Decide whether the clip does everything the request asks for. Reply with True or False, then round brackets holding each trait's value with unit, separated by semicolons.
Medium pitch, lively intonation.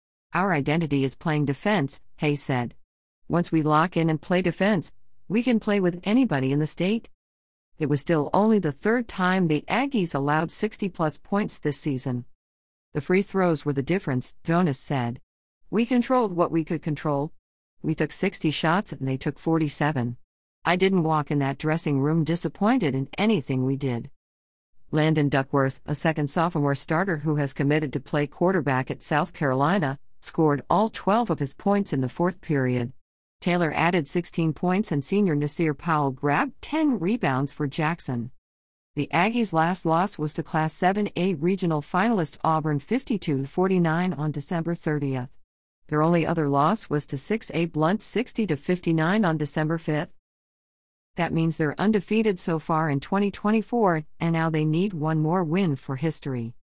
False (155 Hz; 4.4 semitones)